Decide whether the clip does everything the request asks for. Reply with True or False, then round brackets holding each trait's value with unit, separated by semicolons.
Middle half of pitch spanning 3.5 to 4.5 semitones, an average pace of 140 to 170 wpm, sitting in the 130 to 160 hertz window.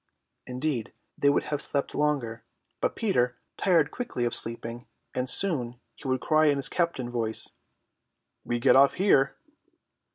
True (3.9 semitones; 150 wpm; 135 Hz)